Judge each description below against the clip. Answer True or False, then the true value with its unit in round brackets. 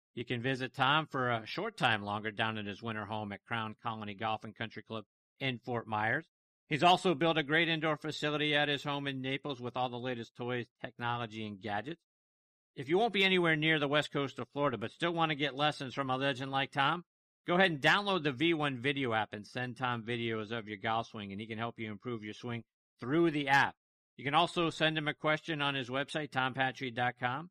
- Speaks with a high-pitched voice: False (130 Hz)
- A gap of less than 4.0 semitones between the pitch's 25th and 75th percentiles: False (4.8 semitones)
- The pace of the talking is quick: True (225 wpm)